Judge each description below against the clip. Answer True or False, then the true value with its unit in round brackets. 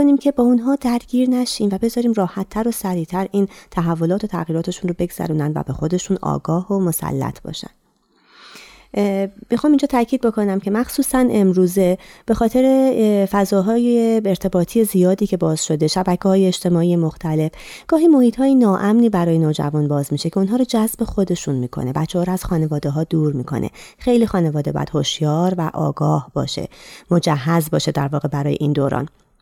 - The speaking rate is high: True (160 wpm)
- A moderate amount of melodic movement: False (6.0 semitones)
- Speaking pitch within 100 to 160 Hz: False (185 Hz)